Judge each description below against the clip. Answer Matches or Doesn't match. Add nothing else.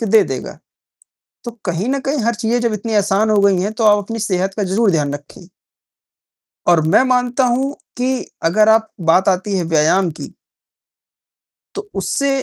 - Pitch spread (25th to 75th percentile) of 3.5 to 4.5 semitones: Matches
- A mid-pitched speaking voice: Doesn't match